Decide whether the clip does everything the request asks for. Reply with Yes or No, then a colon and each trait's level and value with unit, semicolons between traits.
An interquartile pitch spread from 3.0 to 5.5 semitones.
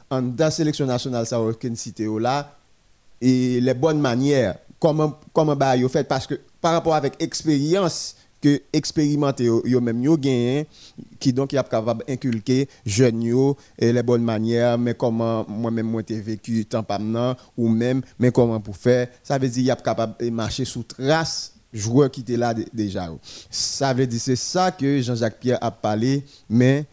Yes: average, 3.3 semitones